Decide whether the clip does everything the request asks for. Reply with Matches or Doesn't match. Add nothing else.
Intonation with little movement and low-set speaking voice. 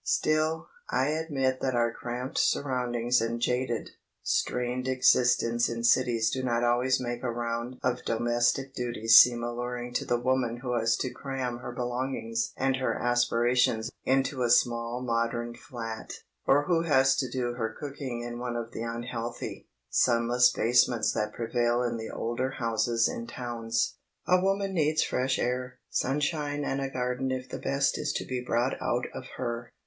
Matches